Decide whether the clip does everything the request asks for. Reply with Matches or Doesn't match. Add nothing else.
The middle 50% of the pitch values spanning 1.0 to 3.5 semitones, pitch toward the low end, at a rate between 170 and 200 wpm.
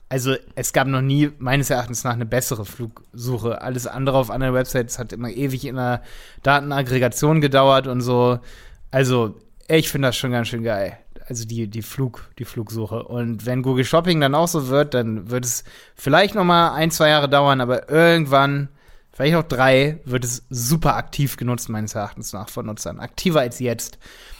Matches